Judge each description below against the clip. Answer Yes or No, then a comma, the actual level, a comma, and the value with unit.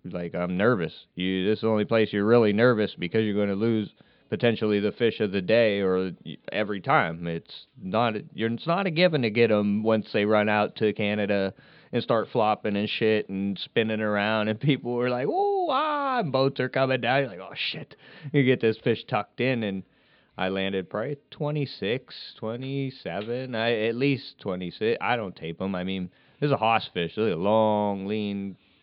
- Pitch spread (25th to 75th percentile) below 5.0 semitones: Yes, average, 3.8 semitones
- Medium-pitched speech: No, low, 110 Hz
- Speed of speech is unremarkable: Yes, average, 195 wpm